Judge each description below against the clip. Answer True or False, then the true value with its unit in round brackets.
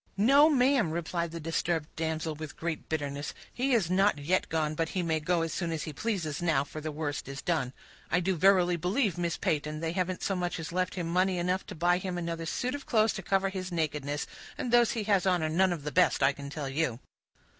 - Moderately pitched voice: True (170 Hz)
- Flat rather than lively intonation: False (3.3 semitones)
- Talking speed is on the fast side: True (235 wpm)